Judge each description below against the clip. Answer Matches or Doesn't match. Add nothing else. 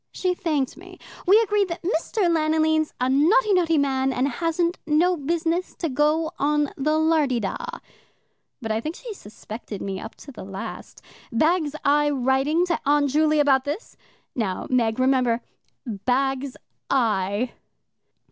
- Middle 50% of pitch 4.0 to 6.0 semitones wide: Matches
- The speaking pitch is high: Matches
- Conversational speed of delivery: Matches